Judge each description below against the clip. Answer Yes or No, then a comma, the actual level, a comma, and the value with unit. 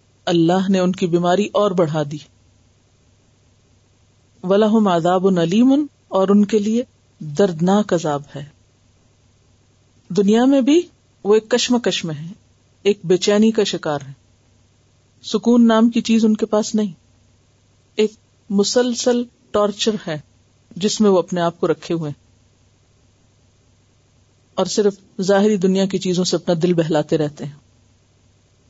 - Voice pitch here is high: No, medium, 170 Hz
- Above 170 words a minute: No, average, 135 wpm